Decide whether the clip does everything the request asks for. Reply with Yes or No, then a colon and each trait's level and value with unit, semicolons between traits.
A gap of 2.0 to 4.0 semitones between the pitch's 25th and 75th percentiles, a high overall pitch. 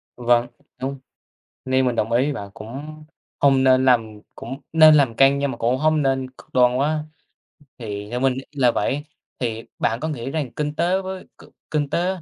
No: average, 3.5 semitones; low, 135 Hz